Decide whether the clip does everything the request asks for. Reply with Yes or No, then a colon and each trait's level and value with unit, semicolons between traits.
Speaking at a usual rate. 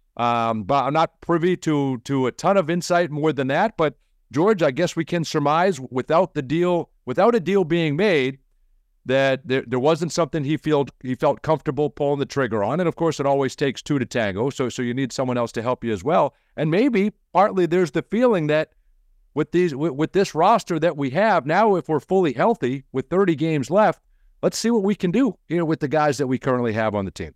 No: fast, 230 wpm